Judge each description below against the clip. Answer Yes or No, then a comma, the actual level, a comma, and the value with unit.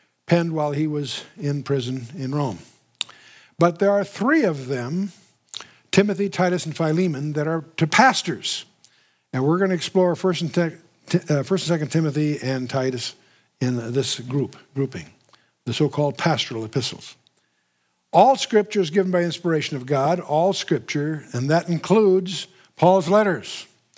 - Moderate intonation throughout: Yes, average, 4.5 semitones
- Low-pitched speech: No, medium, 160 Hz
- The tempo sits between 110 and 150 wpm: Yes, average, 140 wpm